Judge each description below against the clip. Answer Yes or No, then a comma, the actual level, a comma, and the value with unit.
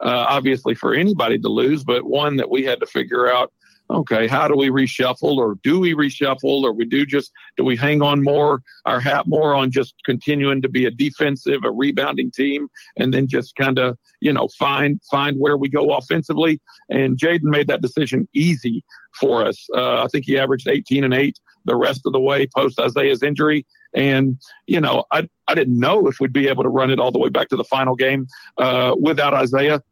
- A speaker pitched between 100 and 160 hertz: Yes, low, 135 Hz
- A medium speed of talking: No, fast, 215 wpm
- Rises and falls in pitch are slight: Yes, narrow, 1.8 semitones